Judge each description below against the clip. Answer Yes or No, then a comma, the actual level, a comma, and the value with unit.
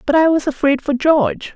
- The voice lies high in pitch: Yes, very high, 290 Hz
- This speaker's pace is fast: Yes, fast, 230 wpm